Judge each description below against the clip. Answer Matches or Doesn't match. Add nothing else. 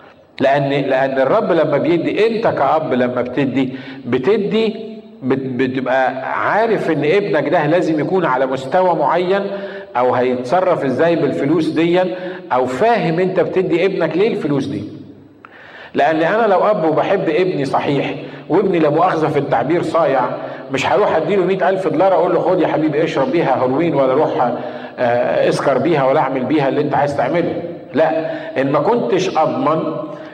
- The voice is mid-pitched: Matches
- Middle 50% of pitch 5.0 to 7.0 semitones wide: Matches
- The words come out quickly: Matches